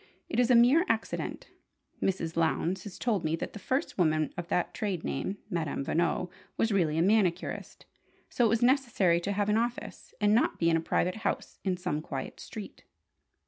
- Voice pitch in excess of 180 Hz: Yes, high, 190 Hz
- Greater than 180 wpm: Yes, average, 190 wpm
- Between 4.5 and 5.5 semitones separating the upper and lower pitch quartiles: Yes, average, 4.9 semitones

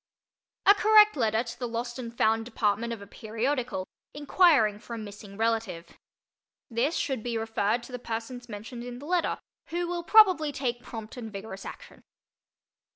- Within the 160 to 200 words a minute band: Yes, average, 165 wpm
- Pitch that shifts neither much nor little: Yes, average, 3.6 semitones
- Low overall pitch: No, high, 235 Hz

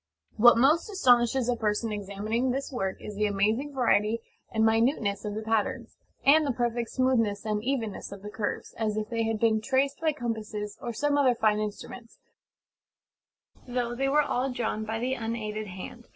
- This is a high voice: Yes, high, 230 Hz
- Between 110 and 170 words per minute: No, average, 180 wpm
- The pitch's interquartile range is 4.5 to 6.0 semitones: No, average, 3.1 semitones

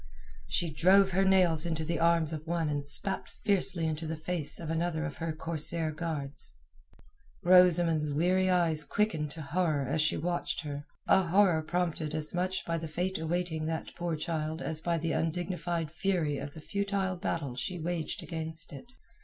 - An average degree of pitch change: No, narrow, 2.3 semitones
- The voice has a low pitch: No, medium, 165 Hz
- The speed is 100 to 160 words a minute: No, average, 170 wpm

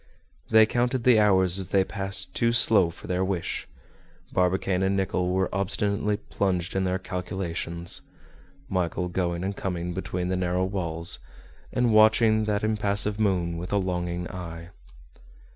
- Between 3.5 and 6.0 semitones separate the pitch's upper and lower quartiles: No, narrow, 2.4 semitones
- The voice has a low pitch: Yes, very low, 95 Hz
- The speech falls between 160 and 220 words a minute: No, average, 145 wpm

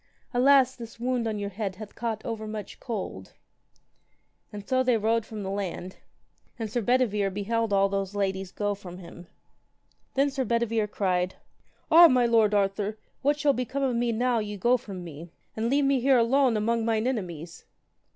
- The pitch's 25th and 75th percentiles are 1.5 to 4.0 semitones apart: Yes, average, 3.7 semitones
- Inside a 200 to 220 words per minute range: No, average, 180 wpm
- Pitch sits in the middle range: No, high, 220 Hz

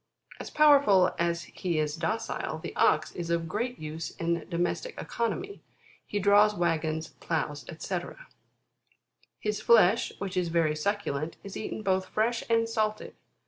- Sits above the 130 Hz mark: Yes, medium, 185 Hz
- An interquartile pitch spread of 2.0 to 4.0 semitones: No, average, 4.5 semitones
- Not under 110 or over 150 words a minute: Yes, average, 145 wpm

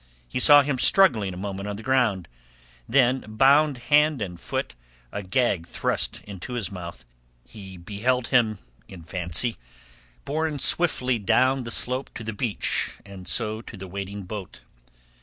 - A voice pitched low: Yes, low, 110 Hz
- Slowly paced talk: No, average, 155 wpm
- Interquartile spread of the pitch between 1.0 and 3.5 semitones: No, average, 5.0 semitones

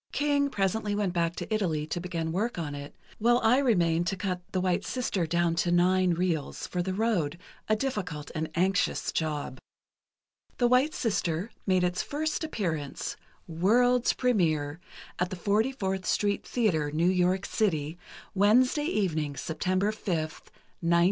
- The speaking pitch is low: No, medium, 185 Hz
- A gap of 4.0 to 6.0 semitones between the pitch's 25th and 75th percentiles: Yes, average, 4.6 semitones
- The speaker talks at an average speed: Yes, average, 150 wpm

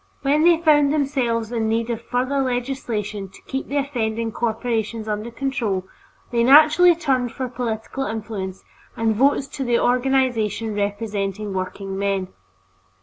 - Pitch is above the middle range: Yes, high, 235 Hz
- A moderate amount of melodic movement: Yes, average, 4.0 semitones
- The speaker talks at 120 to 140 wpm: Yes, slow, 135 wpm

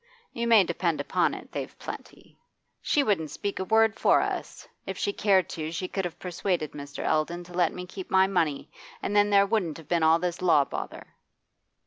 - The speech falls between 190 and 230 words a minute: Yes, average, 200 wpm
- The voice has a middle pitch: Yes, medium, 180 Hz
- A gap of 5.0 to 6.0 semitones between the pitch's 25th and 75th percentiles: No, average, 3.5 semitones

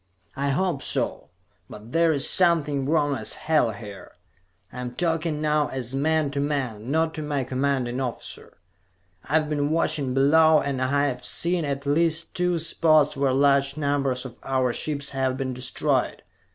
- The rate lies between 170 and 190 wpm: No, average, 155 wpm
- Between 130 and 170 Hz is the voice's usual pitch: Yes, medium, 140 Hz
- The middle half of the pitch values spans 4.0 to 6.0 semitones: No, average, 2.9 semitones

